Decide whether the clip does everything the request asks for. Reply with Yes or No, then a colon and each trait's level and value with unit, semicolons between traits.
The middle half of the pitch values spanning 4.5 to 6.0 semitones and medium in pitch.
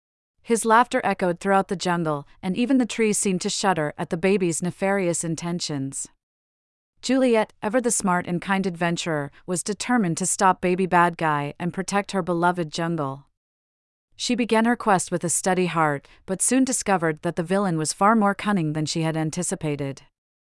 No: average, 4.0 semitones; medium, 180 Hz